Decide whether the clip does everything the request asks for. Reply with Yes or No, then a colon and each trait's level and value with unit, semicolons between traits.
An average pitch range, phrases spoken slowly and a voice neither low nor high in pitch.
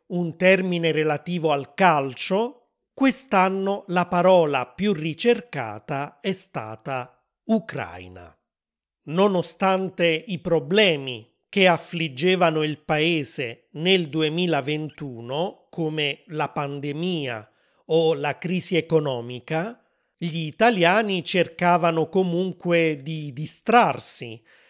Yes: average, 4.1 semitones; slow, 85 wpm; medium, 165 Hz